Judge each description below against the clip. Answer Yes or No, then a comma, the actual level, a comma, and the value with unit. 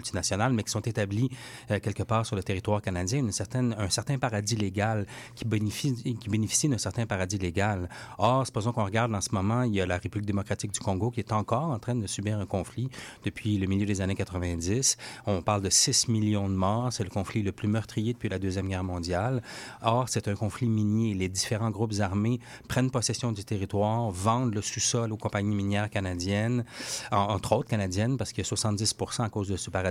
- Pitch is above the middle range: No, low, 110 Hz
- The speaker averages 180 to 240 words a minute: Yes, average, 215 wpm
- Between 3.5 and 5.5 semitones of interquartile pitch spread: No, average, 2.8 semitones